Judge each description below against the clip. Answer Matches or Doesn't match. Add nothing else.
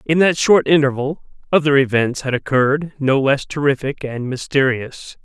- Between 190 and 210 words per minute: Doesn't match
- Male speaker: Matches